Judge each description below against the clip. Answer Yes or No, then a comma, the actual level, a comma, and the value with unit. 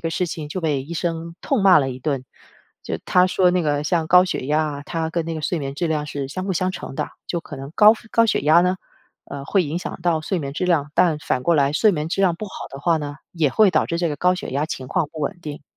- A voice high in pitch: No, medium, 165 Hz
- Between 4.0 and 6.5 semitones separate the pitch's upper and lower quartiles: No, average, 3.6 semitones